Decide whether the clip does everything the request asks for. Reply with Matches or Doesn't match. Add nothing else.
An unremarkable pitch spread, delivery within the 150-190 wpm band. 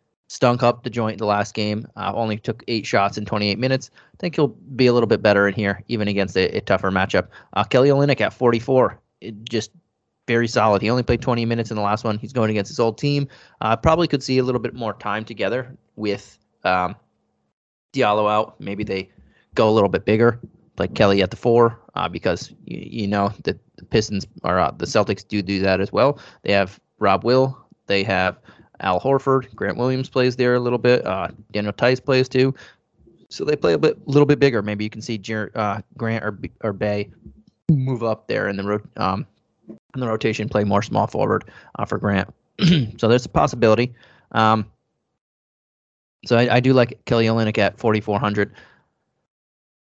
Doesn't match